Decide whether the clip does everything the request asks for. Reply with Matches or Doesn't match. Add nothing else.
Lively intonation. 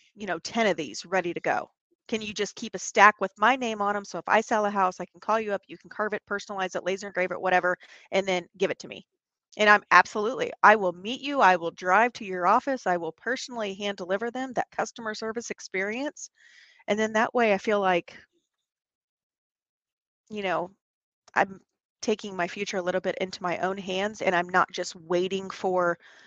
Doesn't match